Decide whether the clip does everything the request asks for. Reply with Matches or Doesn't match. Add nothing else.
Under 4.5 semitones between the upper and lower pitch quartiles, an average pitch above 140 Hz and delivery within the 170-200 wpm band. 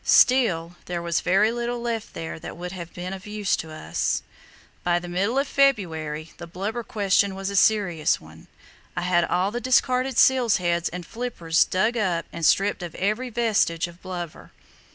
Doesn't match